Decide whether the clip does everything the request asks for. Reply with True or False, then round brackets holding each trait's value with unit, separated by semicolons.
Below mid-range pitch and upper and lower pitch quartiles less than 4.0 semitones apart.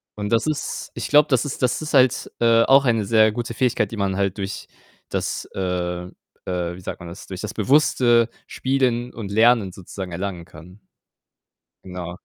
False (110 Hz; 4.5 semitones)